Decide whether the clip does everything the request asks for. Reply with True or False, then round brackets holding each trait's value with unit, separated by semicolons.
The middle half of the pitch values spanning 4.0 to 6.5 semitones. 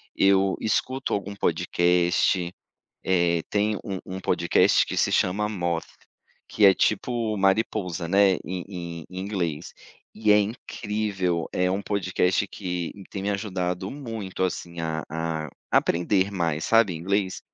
False (2.8 semitones)